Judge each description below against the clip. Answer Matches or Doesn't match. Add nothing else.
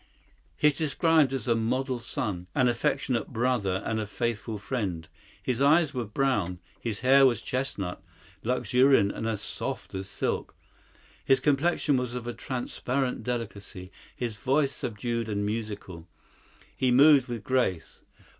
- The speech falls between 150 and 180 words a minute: Doesn't match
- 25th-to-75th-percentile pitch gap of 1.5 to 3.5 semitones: Doesn't match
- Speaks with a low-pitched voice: Matches